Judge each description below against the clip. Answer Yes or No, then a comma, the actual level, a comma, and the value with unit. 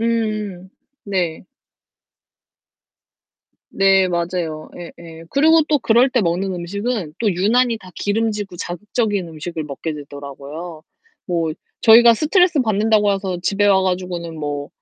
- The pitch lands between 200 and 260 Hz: No, high, 190 Hz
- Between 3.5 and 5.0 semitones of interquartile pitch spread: Yes, average, 4.5 semitones